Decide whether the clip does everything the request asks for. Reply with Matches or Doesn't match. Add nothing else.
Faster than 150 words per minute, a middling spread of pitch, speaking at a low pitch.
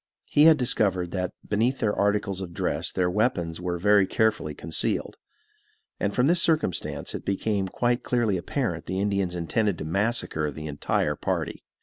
Matches